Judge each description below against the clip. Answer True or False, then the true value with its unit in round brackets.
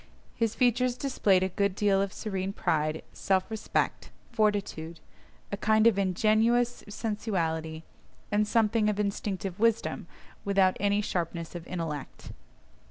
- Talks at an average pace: False (125 wpm)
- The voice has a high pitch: True (200 Hz)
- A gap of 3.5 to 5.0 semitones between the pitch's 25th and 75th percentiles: False (3.0 semitones)